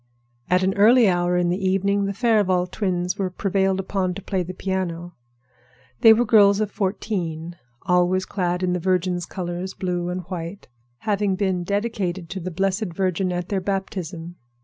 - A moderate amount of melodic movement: No, narrow, 1.9 semitones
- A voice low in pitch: No, medium, 185 Hz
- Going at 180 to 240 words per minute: No, average, 170 wpm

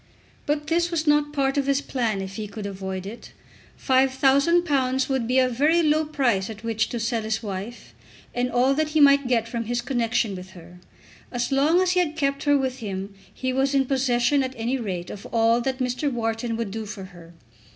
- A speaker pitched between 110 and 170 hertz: No, very high, 250 Hz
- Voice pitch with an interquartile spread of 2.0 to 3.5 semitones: No, average, 4.0 semitones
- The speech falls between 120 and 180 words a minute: No, fast, 205 wpm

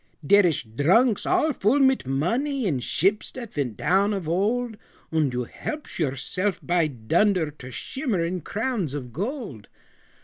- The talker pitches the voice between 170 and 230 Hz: Yes, medium, 185 Hz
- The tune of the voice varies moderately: No, wide, 8.4 semitones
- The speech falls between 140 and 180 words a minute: Yes, average, 145 wpm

